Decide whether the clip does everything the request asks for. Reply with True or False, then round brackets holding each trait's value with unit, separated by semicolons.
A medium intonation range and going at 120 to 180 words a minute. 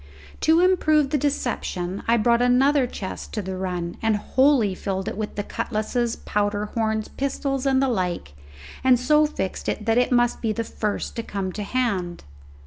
True (4.5 semitones; 175 wpm)